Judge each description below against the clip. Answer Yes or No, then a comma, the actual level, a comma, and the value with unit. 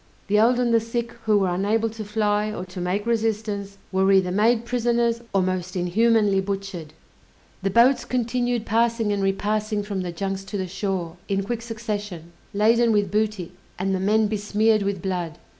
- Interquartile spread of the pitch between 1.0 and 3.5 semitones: Yes, average, 2.8 semitones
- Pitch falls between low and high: No, high, 205 Hz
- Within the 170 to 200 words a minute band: Yes, average, 175 wpm